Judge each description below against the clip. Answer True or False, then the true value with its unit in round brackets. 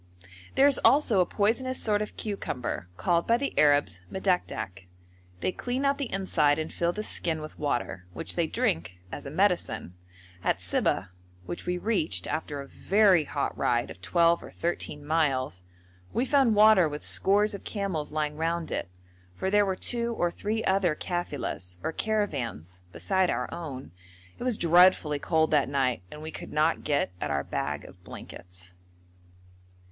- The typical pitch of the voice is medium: True (165 Hz)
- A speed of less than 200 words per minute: True (170 wpm)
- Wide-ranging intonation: True (6.7 semitones)